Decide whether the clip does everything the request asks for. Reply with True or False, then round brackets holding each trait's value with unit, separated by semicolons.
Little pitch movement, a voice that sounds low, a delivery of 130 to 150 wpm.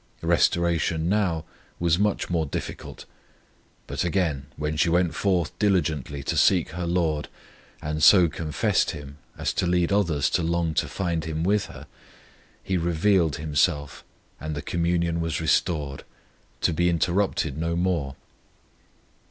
True (2.3 semitones; 85 Hz; 140 wpm)